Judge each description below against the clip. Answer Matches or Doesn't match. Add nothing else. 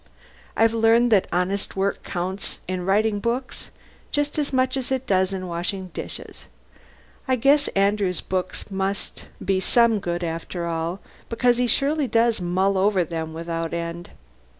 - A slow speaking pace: Doesn't match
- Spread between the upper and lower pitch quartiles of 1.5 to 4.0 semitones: Doesn't match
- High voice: Matches